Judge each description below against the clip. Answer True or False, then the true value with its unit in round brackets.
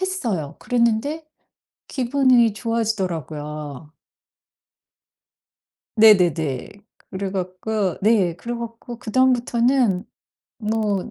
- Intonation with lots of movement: False (4.8 semitones)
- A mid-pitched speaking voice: False (220 Hz)